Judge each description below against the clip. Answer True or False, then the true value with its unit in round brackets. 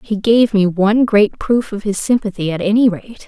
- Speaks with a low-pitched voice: False (210 Hz)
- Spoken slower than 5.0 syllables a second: False (5.1 syllables/s)